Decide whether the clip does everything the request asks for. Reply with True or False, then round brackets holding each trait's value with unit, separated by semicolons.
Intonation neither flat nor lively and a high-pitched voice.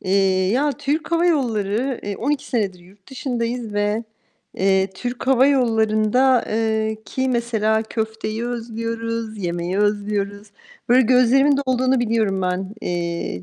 True (3.7 semitones; 225 Hz)